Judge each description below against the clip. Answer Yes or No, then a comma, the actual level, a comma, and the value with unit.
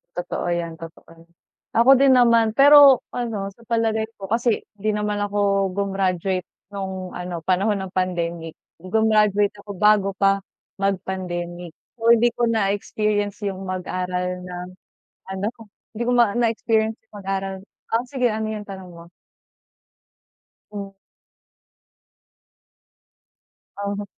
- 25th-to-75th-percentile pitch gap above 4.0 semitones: No, average, 3.1 semitones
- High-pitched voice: Yes, high, 200 Hz